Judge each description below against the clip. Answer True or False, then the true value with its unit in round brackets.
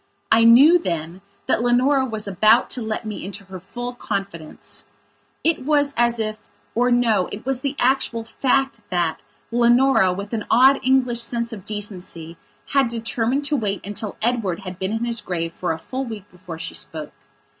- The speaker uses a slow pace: False (170 wpm)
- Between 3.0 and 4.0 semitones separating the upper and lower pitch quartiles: False (4.4 semitones)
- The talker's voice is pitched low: False (225 Hz)